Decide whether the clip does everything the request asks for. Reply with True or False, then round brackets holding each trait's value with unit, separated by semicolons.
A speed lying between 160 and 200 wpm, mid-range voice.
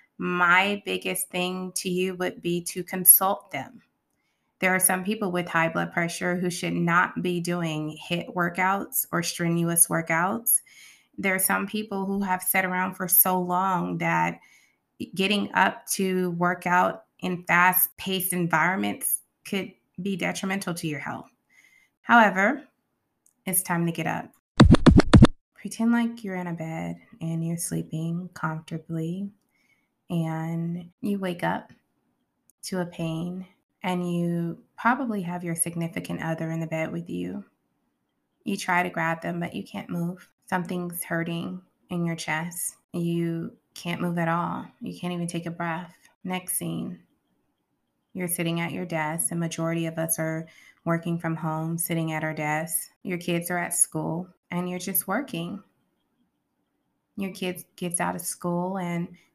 False (150 wpm; 175 Hz)